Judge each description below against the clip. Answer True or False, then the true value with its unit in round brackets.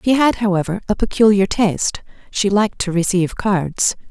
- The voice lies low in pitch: False (200 Hz)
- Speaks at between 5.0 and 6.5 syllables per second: True (5.3 syllables/s)